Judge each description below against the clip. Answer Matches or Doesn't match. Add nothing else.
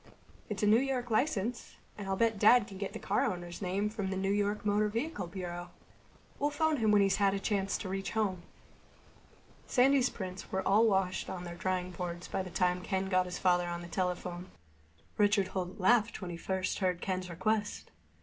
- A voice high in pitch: Matches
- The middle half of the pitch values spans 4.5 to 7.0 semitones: Doesn't match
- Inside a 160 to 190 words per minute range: Doesn't match